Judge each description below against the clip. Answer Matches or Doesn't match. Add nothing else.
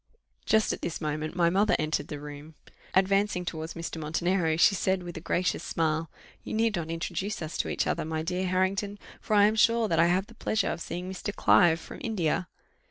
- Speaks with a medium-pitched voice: Matches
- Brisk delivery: Matches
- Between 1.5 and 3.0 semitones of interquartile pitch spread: Doesn't match